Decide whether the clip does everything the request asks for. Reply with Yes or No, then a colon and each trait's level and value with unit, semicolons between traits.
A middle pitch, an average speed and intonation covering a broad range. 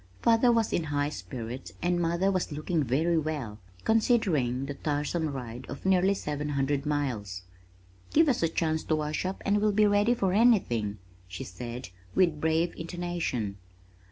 Yes: medium, 155 Hz; average, 160 wpm; wide, 5.7 semitones